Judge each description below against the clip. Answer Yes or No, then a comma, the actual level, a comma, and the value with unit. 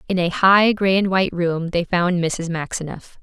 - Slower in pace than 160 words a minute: No, fast, 205 wpm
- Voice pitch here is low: No, medium, 180 Hz